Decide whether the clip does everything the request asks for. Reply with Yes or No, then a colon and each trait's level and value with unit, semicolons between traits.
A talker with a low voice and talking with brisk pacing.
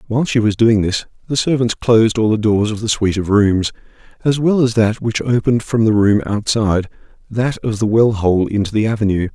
Yes: low, 110 Hz; fast, 210 wpm